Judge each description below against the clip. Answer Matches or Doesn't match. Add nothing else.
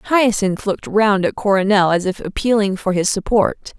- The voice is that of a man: Doesn't match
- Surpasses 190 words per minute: Doesn't match